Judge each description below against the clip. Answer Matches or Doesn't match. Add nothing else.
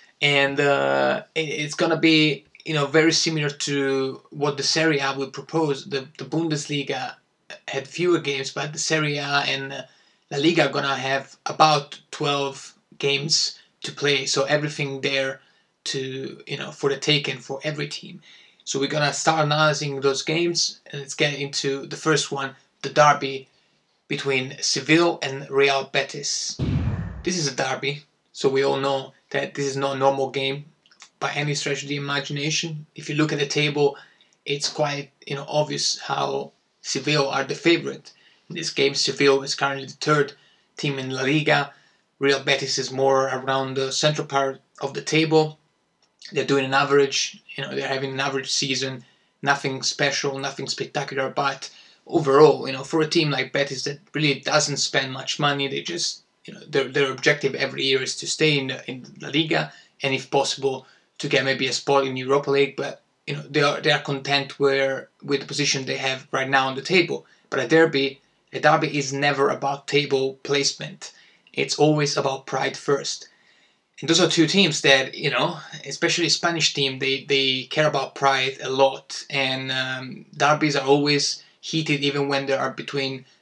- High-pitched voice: Doesn't match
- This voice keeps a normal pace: Doesn't match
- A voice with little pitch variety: Matches